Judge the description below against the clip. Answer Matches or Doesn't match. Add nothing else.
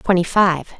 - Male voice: Doesn't match